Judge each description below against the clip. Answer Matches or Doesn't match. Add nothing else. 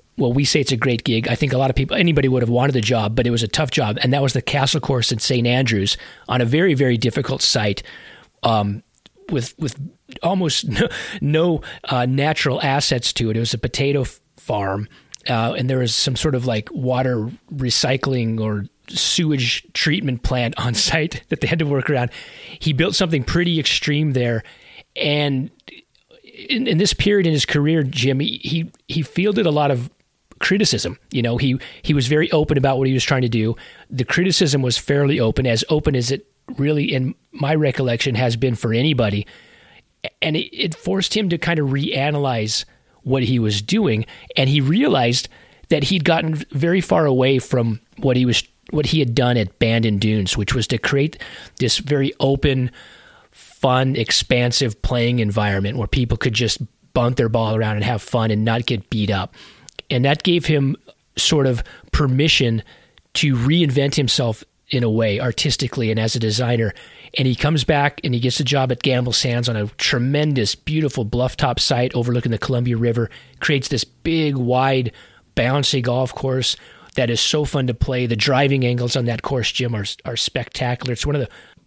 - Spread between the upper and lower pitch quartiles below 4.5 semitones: Matches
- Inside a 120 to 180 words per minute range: Doesn't match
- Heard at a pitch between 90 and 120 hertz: Doesn't match